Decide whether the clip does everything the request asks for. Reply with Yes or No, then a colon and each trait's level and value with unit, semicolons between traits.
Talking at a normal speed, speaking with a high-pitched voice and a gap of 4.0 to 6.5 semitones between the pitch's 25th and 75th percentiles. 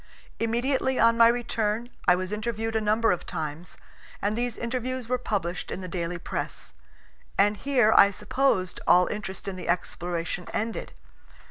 Yes: average, 155 wpm; high, 215 Hz; average, 4.3 semitones